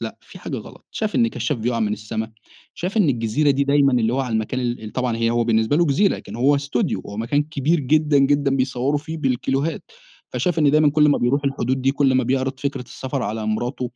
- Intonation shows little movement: No, average, 3.4 semitones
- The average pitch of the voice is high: No, low, 135 Hz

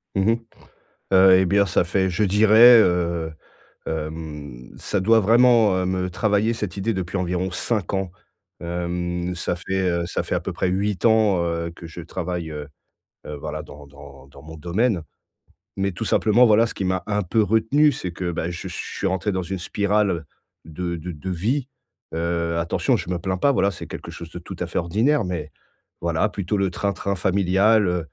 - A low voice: Yes, very low, 90 Hz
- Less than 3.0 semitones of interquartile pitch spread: No, average, 3.3 semitones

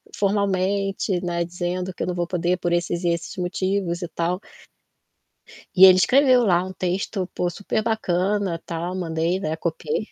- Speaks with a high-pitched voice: No, medium, 180 Hz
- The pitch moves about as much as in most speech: No, narrow, 2.1 semitones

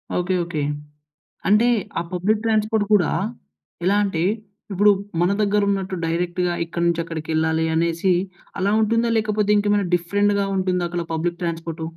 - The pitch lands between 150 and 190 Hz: Yes, medium, 185 Hz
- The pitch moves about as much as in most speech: Yes, average, 3.4 semitones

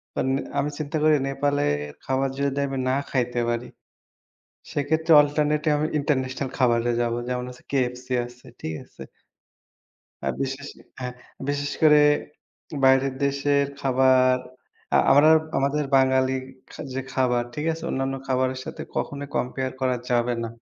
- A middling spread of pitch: No, narrow, 2.1 semitones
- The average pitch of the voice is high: No, low, 135 Hz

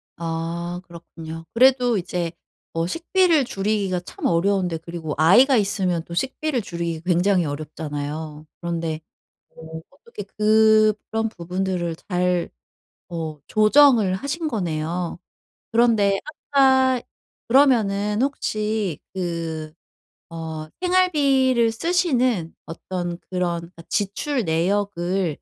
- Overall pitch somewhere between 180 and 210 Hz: Yes, medium, 185 Hz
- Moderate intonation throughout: No, wide, 5.7 semitones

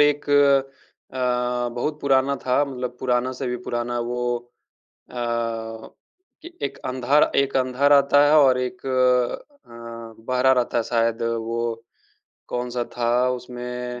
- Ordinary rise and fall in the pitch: No, narrow, 1.8 semitones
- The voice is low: Yes, low, 125 Hz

